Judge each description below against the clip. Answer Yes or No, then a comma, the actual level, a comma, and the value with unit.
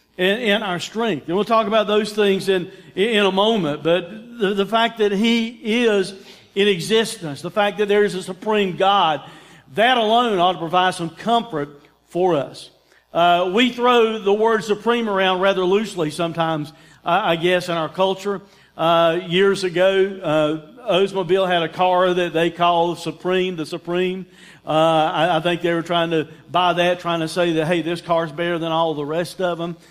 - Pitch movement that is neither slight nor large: Yes, average, 3.2 semitones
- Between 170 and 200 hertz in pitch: Yes, medium, 185 Hz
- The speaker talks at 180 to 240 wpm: Yes, average, 185 wpm